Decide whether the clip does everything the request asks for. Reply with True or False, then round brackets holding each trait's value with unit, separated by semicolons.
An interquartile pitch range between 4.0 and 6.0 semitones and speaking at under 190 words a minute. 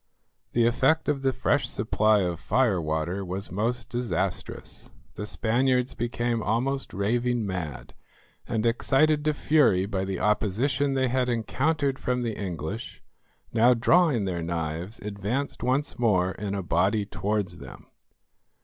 True (5.0 semitones; 140 wpm)